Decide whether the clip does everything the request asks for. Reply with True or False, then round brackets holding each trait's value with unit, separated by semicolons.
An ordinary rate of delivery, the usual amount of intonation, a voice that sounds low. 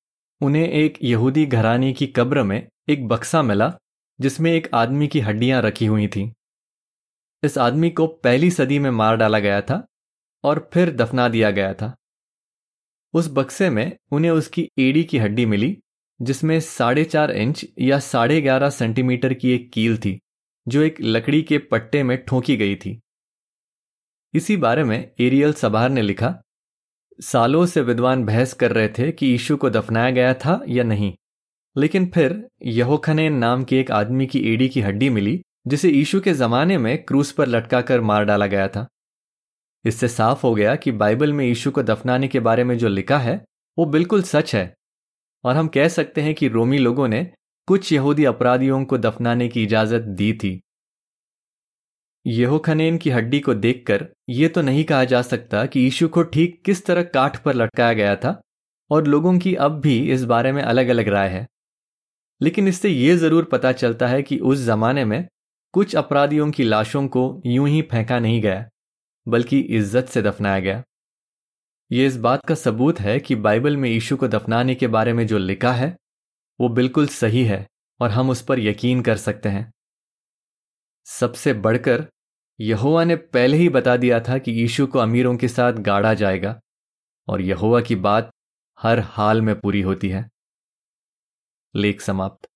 True (175 wpm; 4.4 semitones; 125 Hz)